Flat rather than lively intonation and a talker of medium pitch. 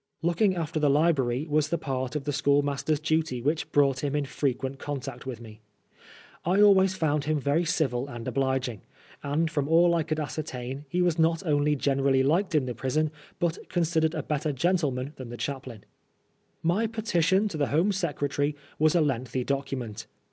No: average, 3.4 semitones; medium, 145 Hz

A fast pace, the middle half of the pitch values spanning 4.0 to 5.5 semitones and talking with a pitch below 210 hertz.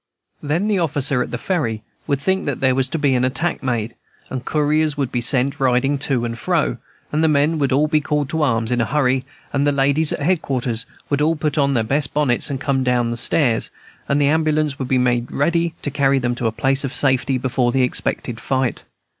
No: fast, 225 wpm; average, 3.1 semitones; low, 135 Hz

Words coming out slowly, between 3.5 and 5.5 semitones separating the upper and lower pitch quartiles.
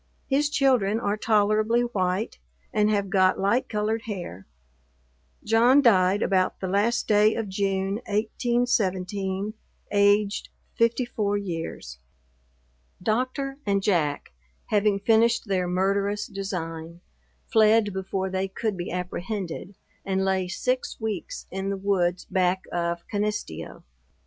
No: slow, 115 wpm; average, 2.7 semitones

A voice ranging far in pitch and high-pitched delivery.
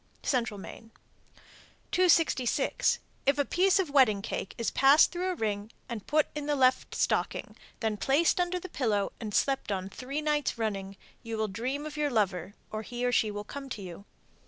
Yes: wide, 5.9 semitones; high, 245 Hz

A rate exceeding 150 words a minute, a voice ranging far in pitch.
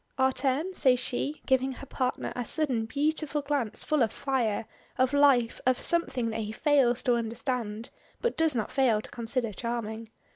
No: average, 175 wpm; average, 3.6 semitones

